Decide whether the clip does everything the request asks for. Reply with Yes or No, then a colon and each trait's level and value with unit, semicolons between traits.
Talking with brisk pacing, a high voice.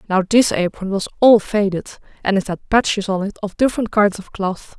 Yes: fast, 215 wpm; high, 200 Hz